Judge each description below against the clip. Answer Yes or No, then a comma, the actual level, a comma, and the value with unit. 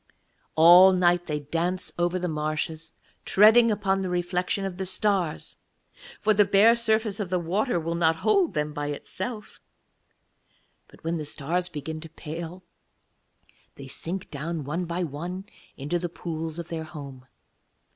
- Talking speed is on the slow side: No, average, 155 wpm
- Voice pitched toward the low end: No, medium, 175 Hz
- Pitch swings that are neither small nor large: Yes, average, 3.3 semitones